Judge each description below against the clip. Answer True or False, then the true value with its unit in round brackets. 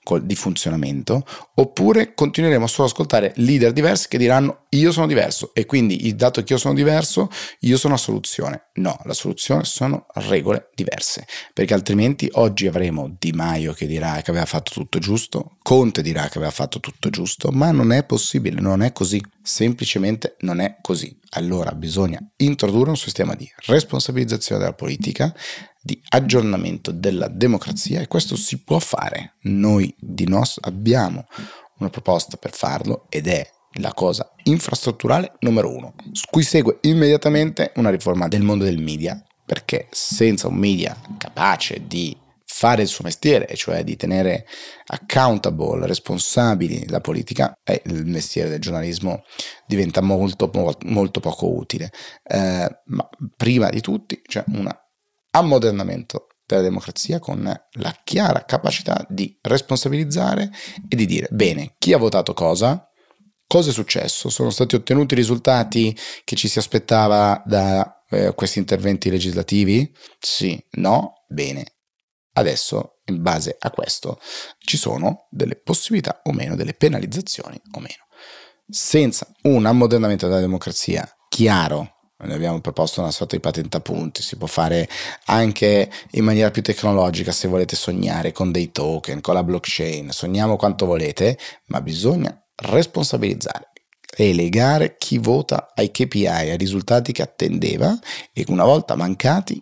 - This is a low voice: True (110 Hz)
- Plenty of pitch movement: True (6.6 semitones)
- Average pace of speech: True (145 wpm)